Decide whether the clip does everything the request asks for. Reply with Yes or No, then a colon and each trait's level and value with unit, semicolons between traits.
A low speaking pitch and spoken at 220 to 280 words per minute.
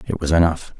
Yes: very low, 80 Hz; fast, 225 wpm